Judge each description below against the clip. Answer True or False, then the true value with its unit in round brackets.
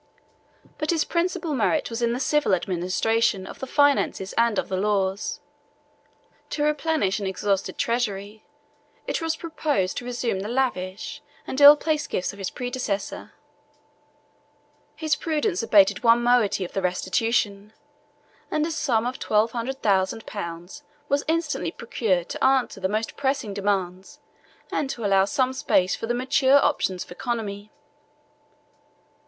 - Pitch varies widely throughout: True (5.7 semitones)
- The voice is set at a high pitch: True (230 Hz)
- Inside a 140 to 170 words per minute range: True (145 wpm)